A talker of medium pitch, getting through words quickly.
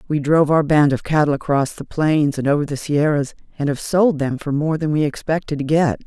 Yes: medium, 150 Hz; fast, 240 wpm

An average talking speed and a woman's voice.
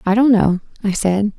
No: fast, 215 wpm; female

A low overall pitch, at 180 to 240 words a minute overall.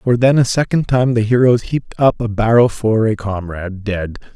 Yes: low, 115 Hz; fast, 205 wpm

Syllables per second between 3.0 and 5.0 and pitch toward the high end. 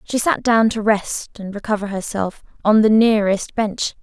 Yes: 4.6 syllables/s; high, 210 Hz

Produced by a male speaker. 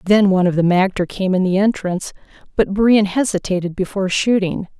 No: female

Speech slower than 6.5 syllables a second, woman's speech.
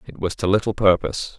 No: 6.2 syllables/s; male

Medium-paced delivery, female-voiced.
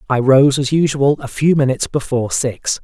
No: average, 190 wpm; male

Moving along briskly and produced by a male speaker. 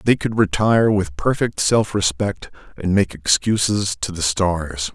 No: average, 160 wpm; male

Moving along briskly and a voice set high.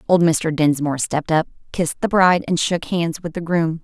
No: fast, 220 wpm; medium, 165 Hz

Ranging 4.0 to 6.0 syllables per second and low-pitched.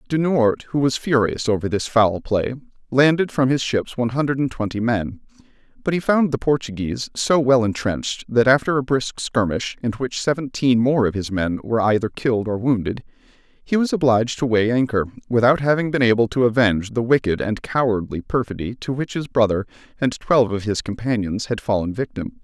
Yes: 5.5 syllables/s; low, 120 Hz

